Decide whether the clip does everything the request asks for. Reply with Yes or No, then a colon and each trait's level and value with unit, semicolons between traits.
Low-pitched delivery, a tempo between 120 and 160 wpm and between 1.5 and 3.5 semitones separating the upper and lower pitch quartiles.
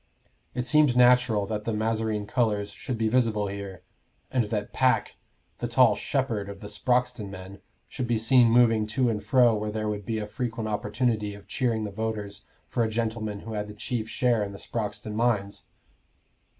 No: low, 110 Hz; average, 185 wpm; narrow, 2.5 semitones